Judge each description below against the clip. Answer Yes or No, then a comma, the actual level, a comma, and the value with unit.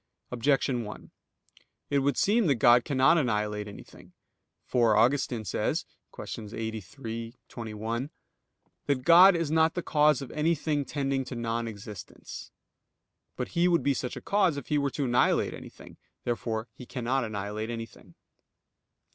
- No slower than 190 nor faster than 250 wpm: No, average, 145 wpm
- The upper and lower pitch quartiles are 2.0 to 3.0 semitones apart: No, average, 4.3 semitones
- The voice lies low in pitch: Yes, low, 125 Hz